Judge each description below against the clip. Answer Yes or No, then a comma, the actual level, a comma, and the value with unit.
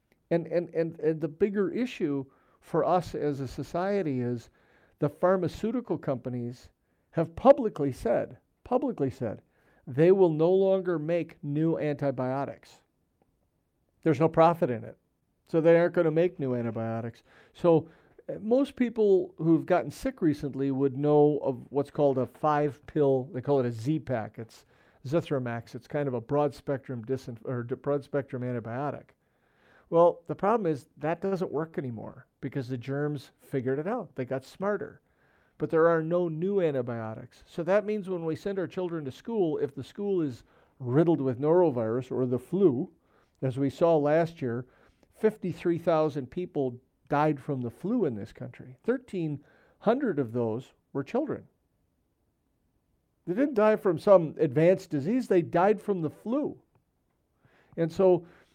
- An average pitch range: Yes, average, 4.9 semitones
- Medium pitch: Yes, medium, 155 Hz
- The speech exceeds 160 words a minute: No, average, 155 wpm